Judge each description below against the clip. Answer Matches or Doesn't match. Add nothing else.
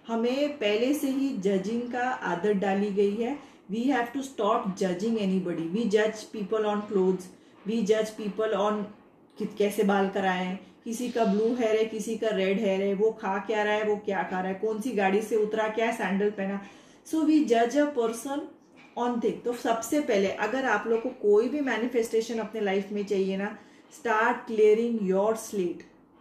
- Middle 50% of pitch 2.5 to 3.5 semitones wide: Matches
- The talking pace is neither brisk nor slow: Matches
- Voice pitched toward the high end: Matches